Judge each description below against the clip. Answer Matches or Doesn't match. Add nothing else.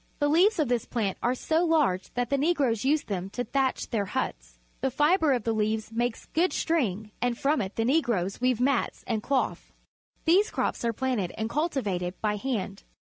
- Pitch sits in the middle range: Doesn't match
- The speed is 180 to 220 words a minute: Matches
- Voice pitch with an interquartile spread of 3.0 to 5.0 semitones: Doesn't match